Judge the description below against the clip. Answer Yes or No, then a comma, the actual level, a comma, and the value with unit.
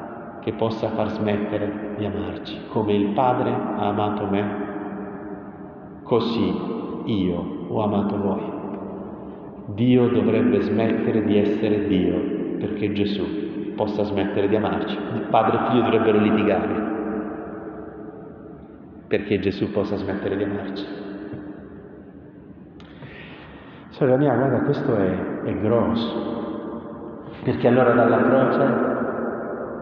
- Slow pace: Yes, slow, 105 wpm